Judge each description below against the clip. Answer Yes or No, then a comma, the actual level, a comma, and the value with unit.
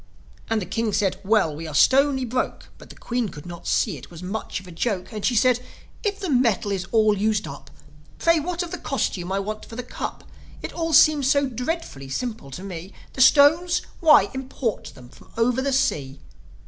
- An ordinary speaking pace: No, fast, 210 wpm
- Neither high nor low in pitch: No, high, 225 Hz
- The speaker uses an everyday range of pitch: No, wide, 6.4 semitones